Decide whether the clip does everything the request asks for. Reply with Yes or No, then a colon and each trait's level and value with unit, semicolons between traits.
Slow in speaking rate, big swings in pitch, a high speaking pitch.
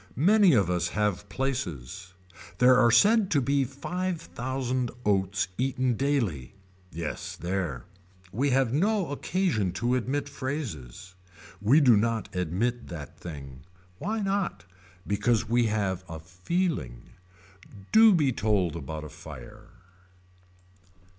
No: slow, 120 wpm; wide, 7.5 semitones; low, 115 Hz